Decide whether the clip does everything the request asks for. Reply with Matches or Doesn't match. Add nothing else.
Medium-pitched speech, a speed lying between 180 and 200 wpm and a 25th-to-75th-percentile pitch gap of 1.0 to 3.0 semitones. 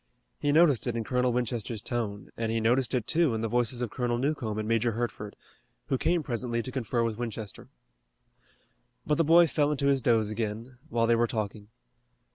Doesn't match